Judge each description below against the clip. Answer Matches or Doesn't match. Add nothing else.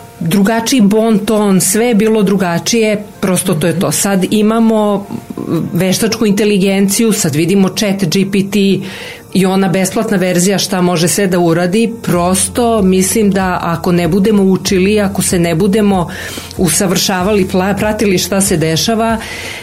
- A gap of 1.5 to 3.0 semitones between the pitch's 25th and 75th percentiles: Matches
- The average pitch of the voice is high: Matches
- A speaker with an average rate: Matches